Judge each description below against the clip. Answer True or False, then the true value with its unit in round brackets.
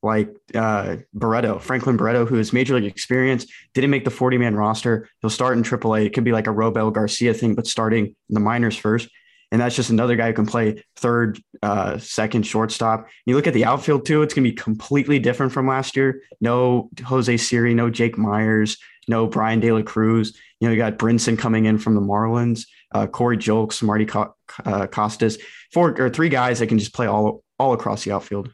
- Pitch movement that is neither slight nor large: False (2.1 semitones)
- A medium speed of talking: False (210 wpm)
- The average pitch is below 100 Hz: False (115 Hz)